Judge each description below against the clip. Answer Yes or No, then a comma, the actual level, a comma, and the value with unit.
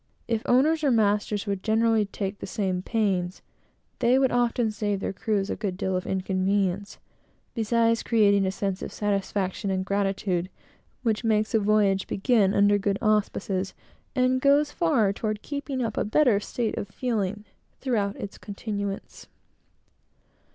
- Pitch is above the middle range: Yes, high, 210 Hz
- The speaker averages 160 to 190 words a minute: No, average, 150 wpm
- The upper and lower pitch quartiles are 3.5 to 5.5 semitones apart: No, average, 2.7 semitones